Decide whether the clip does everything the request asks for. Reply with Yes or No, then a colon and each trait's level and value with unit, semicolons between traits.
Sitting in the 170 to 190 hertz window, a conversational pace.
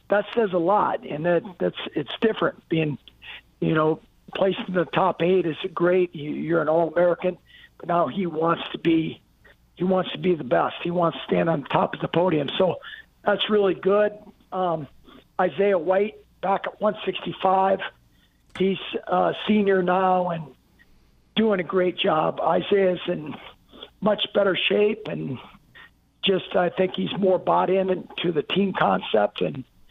Yes: medium, 185 Hz; average, 165 wpm